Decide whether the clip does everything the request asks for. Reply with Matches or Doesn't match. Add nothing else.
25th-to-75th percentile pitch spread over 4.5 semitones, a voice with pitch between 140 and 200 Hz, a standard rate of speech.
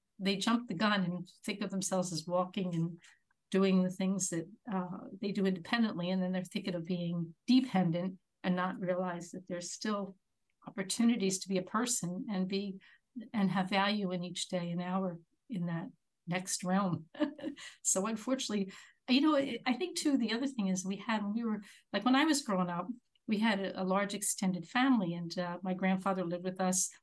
Doesn't match